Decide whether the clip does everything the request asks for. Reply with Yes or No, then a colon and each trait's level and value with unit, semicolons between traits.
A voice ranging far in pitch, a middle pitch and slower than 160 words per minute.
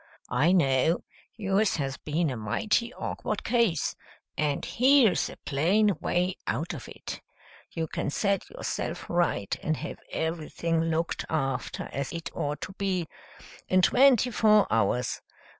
Yes: wide, 5.7 semitones; medium, 165 Hz; average, 140 wpm